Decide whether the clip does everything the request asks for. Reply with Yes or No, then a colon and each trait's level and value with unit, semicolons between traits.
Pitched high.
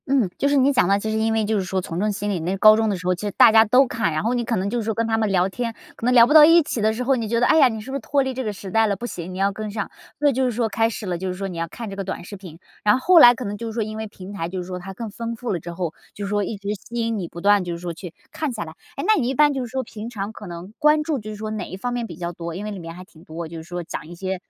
Yes: high, 210 Hz